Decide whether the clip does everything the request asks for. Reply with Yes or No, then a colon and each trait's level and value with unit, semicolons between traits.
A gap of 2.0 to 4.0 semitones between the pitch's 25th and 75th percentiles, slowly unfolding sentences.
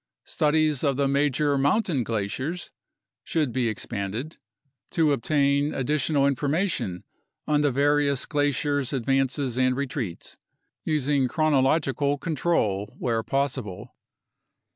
Yes: narrow, 2.6 semitones; slow, 110 wpm